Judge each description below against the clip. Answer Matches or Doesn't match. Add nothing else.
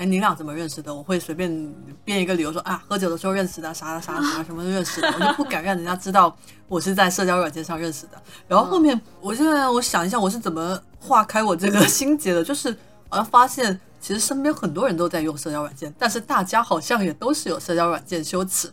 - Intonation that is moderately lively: Matches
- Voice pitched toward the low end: Doesn't match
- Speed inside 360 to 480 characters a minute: Matches